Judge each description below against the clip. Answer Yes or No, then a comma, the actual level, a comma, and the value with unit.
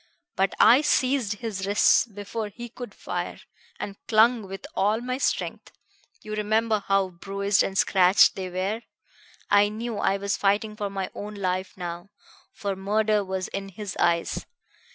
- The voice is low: No, high, 205 Hz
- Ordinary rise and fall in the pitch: No, narrow, 2.1 semitones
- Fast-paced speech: No, average, 155 wpm